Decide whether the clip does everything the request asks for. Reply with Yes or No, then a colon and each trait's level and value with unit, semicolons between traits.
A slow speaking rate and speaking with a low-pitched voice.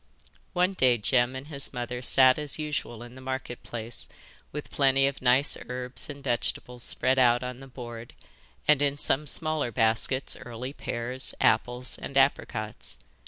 No: average, 160 wpm; low, 130 Hz